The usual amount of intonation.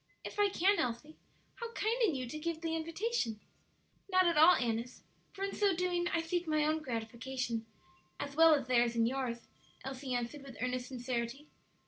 No: wide, 5.8 semitones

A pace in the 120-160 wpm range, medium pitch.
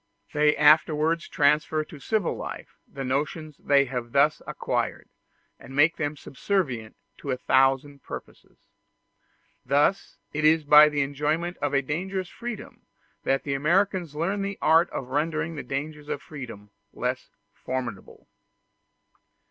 Yes: slow, 135 wpm; medium, 150 Hz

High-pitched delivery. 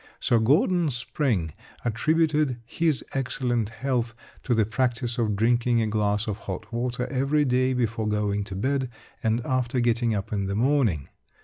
No: low, 120 Hz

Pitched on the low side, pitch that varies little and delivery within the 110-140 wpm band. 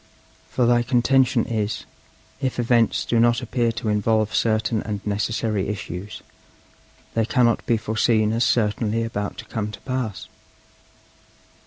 Yes: low, 115 Hz; narrow, 2.0 semitones; slow, 135 wpm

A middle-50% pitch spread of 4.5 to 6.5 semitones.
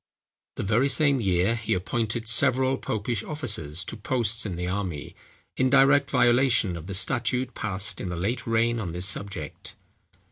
Yes: average, 5.0 semitones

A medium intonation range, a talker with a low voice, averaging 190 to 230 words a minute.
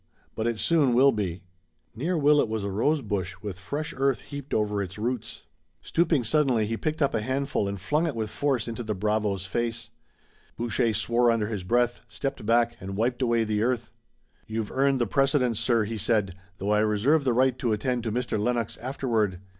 Yes: average, 3.9 semitones; low, 115 Hz; average, 195 wpm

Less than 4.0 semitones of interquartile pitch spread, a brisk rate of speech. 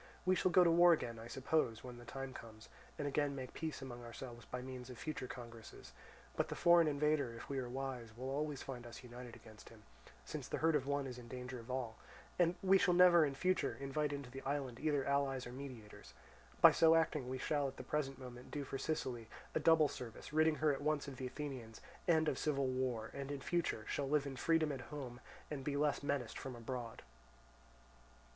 Yes: average, 3.4 semitones; fast, 220 wpm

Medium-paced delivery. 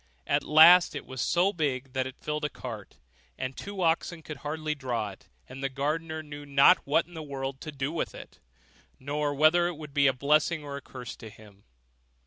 No: fast, 210 wpm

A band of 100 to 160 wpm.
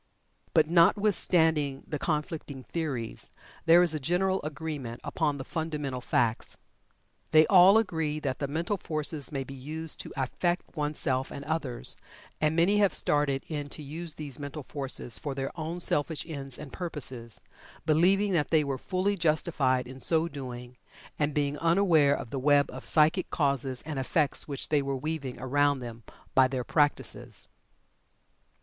Yes: average, 155 wpm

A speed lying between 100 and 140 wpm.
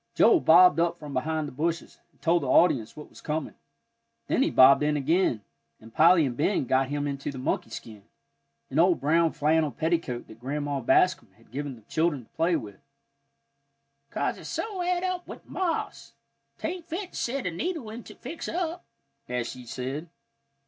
No: average, 185 wpm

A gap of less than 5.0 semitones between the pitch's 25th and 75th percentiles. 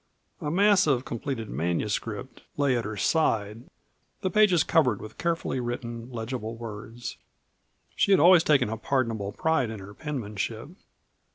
No: wide, 5.5 semitones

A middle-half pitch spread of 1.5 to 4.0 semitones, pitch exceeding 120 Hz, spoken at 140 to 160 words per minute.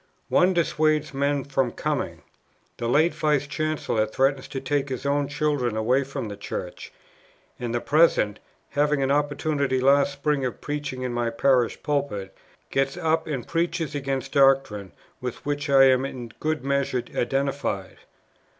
Yes: narrow, 2.4 semitones; medium, 140 Hz; average, 150 wpm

